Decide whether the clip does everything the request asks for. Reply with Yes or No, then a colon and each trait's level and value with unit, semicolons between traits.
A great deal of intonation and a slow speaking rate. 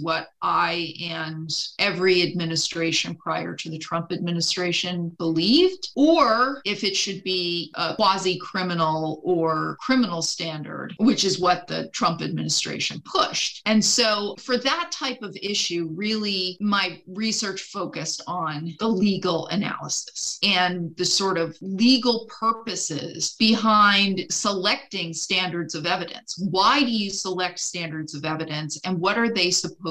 No: average, 3.7 semitones; slow, 130 wpm